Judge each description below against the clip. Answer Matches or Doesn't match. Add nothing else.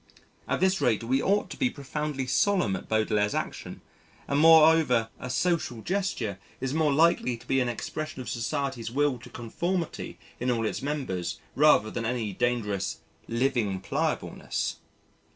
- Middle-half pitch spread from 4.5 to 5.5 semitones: Matches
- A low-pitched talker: Matches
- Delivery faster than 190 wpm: Doesn't match